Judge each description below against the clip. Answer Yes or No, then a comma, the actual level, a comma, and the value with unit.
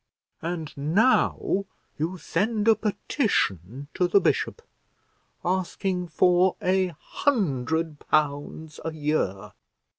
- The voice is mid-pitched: Yes, medium, 170 Hz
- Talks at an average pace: No, slow, 95 wpm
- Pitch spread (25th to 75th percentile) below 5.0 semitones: Yes, average, 4.1 semitones